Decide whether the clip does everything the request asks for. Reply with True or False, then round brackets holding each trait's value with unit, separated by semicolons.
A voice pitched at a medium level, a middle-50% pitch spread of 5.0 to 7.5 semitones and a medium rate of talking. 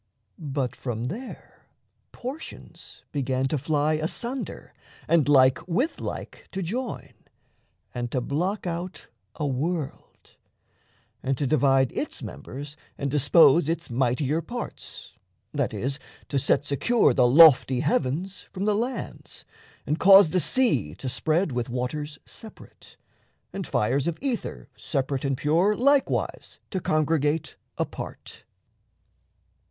False (150 Hz; 5.4 semitones; 125 wpm)